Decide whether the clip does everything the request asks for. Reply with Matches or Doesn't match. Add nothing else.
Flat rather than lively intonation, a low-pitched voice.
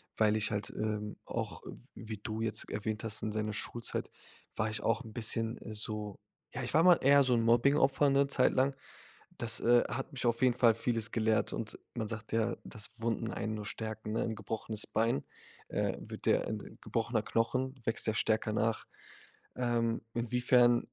Matches